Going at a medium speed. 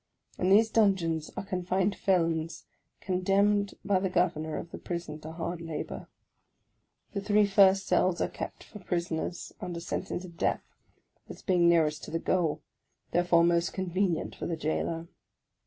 Yes: average, 155 wpm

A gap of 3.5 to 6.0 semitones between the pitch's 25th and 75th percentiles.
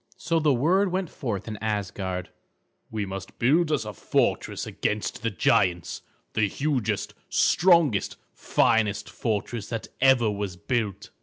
Yes: wide, 5.6 semitones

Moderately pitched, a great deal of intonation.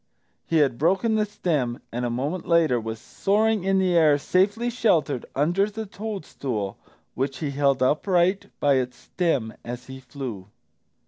Yes: medium, 155 Hz; wide, 7.0 semitones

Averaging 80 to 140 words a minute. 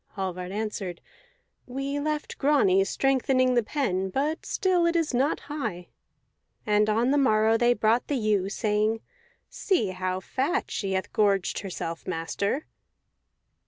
Yes: slow, 135 wpm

